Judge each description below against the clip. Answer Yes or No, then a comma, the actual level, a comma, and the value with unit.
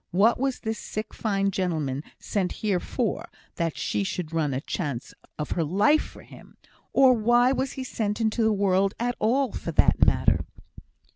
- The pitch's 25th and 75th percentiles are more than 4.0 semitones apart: Yes, average, 5.1 semitones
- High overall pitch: Yes, high, 205 Hz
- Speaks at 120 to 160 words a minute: No, average, 180 wpm